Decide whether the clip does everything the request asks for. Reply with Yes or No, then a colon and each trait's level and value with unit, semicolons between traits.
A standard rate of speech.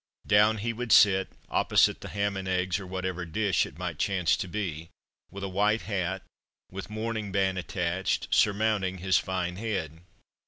Yes: average, 165 wpm